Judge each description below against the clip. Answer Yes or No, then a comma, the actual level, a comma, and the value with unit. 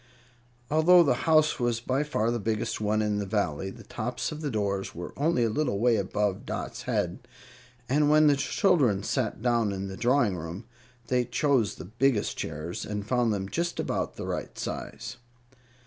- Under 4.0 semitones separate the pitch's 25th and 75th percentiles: No, average, 5.2 semitones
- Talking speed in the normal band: Yes, average, 180 wpm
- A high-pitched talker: No, low, 115 Hz